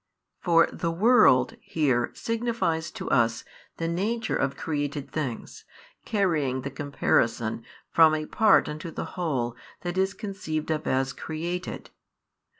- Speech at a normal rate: No, slow, 130 wpm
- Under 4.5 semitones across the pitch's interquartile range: No, average, 4.9 semitones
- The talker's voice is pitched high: No, medium, 155 Hz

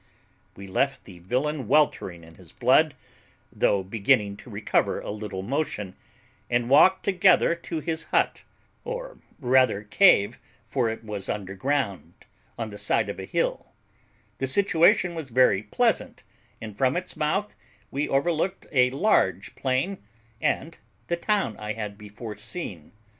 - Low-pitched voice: Yes, low, 130 Hz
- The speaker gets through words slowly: No, average, 145 wpm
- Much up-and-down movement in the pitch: Yes, wide, 7.9 semitones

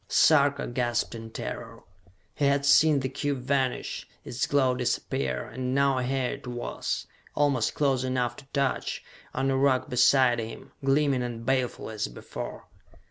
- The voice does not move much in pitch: Yes, narrow, 2.3 semitones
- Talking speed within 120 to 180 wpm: Yes, average, 150 wpm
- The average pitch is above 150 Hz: No, low, 130 Hz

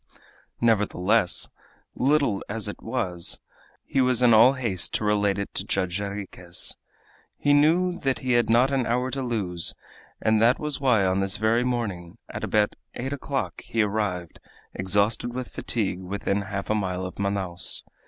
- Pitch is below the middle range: Yes, low, 110 Hz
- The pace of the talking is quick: No, average, 165 wpm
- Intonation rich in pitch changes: No, average, 4.3 semitones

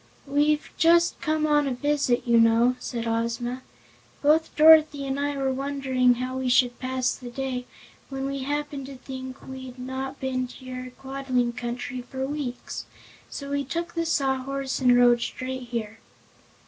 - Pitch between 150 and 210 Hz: No, very high, 260 Hz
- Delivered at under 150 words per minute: No, average, 160 wpm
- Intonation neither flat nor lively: No, narrow, 2.1 semitones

